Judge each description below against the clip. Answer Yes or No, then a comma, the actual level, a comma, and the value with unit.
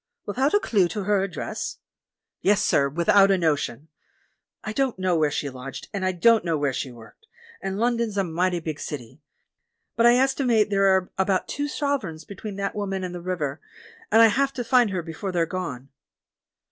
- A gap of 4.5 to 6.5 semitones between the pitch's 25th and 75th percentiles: Yes, average, 5.1 semitones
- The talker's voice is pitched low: No, high, 190 Hz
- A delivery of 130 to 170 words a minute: No, average, 190 wpm